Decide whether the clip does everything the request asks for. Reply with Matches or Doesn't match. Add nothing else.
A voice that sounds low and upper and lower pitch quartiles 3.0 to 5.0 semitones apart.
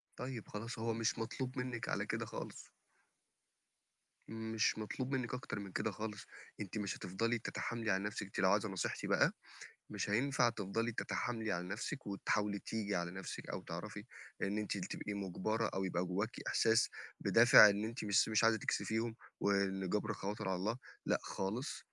Doesn't match